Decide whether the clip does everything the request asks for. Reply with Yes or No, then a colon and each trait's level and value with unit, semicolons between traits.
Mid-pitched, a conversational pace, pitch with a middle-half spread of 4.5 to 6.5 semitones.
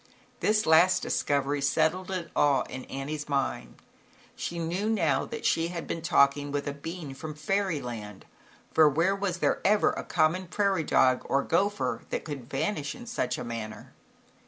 Yes: medium, 155 Hz; average, 165 wpm; average, 4.8 semitones